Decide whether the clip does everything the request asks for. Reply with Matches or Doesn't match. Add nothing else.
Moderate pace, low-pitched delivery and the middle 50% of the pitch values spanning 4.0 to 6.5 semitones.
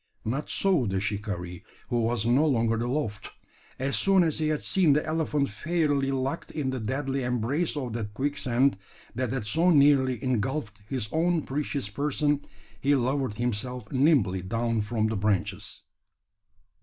Matches